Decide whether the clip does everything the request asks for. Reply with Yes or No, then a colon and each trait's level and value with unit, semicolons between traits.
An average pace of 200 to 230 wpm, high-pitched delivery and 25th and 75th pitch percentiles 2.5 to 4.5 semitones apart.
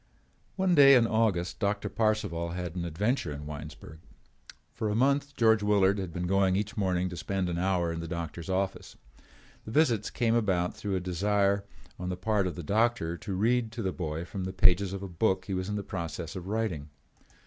No: fast, 205 wpm; very low, 95 Hz; average, 3.5 semitones